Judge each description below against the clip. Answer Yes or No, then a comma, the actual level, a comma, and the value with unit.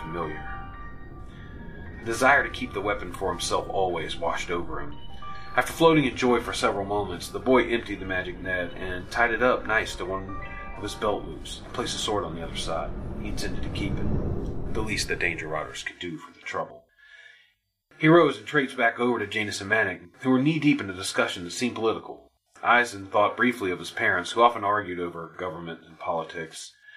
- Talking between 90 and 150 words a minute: No, fast, 205 wpm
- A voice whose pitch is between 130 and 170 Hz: No, low, 100 Hz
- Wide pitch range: Yes, wide, 6.2 semitones